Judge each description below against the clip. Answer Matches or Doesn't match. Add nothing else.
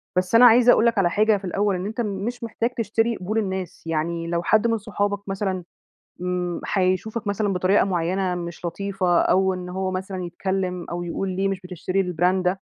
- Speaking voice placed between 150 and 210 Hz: Matches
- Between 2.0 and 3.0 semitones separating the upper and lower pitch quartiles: Matches